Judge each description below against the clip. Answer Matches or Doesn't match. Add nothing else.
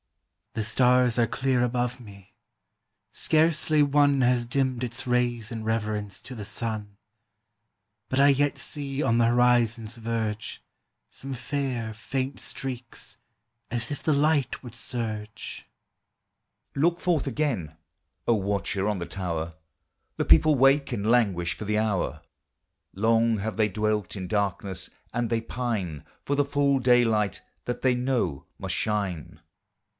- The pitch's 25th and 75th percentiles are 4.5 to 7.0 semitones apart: Doesn't match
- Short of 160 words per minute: Matches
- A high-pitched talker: Doesn't match